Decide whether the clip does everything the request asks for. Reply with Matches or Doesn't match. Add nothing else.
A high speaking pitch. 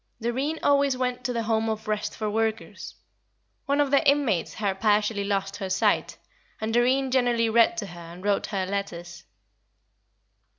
Matches